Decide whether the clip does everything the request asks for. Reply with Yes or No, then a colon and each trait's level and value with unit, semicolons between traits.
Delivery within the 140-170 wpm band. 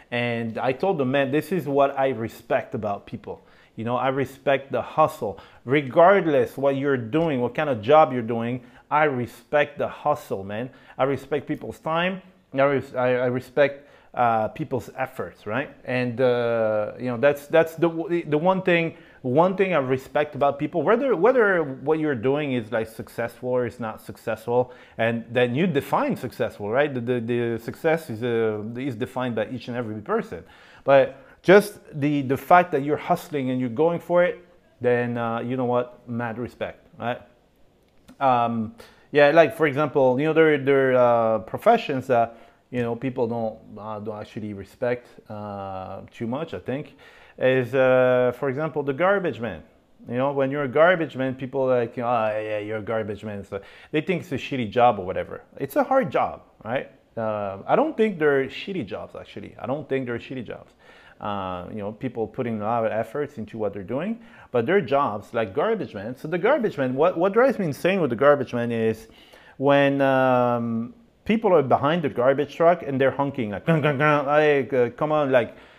No: average, 190 wpm